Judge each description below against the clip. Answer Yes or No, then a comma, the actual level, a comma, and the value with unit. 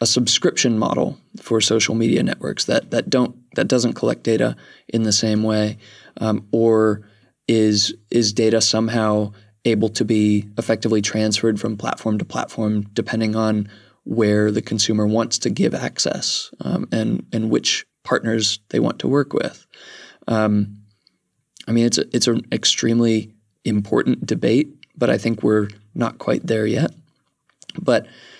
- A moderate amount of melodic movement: No, narrow, 1.3 semitones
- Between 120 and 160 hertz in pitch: No, low, 110 Hz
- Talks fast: No, average, 150 wpm